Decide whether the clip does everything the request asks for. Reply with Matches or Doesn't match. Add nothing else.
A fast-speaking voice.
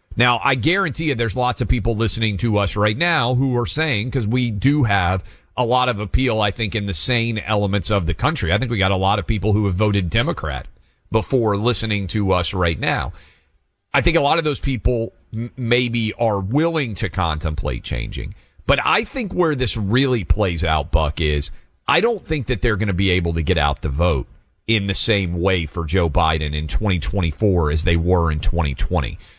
Matches